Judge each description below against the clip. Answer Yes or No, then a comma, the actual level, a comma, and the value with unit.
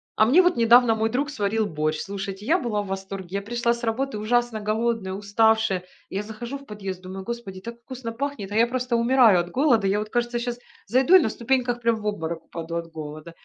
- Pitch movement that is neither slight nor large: Yes, average, 3.6 semitones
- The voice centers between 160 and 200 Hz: No, high, 220 Hz